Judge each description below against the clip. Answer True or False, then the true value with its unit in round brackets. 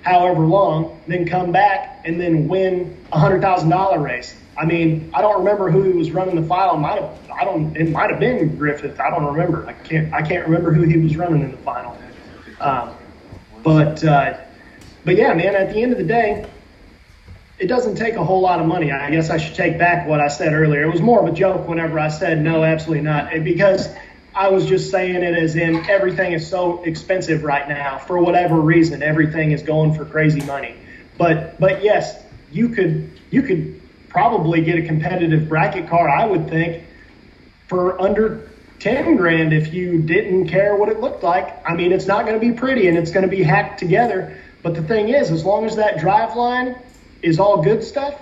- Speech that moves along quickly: True (210 wpm)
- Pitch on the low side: False (170 Hz)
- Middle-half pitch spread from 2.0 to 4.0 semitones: True (3.2 semitones)